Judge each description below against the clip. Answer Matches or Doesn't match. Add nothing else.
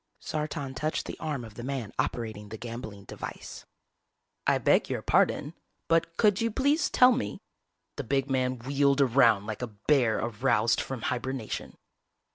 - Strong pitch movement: Doesn't match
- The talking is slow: Doesn't match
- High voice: Doesn't match